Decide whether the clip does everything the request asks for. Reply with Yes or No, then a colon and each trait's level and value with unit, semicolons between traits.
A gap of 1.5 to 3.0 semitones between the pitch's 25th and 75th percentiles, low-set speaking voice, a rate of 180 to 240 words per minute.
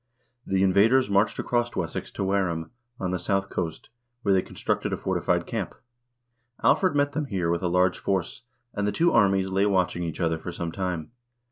Yes: narrow, 2.5 semitones; very low, 95 Hz; average, 190 wpm